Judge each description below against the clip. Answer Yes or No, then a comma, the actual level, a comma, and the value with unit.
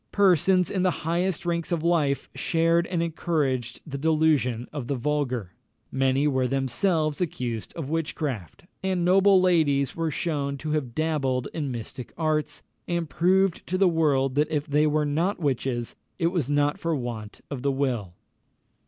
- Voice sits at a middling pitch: Yes, medium, 150 Hz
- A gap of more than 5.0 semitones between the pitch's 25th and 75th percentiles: No, average, 4.1 semitones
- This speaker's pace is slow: No, average, 160 wpm